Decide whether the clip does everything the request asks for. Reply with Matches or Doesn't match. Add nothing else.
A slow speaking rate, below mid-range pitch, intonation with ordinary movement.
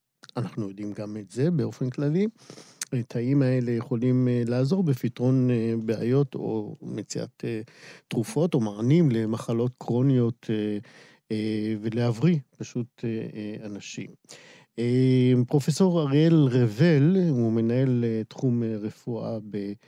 Matches